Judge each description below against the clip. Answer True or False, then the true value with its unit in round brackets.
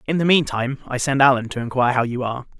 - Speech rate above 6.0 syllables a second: True (7.1 syllables/s)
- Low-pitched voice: True (130 Hz)